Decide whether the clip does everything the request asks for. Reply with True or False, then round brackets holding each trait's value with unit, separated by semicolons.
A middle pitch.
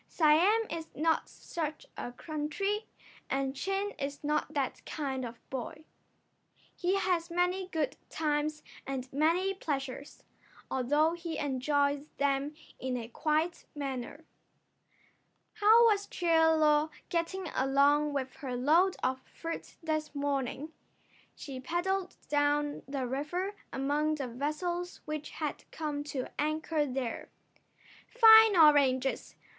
False (300 Hz)